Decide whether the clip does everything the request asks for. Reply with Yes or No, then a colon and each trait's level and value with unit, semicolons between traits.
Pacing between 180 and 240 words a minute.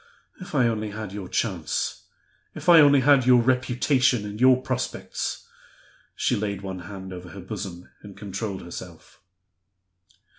No: average, 145 wpm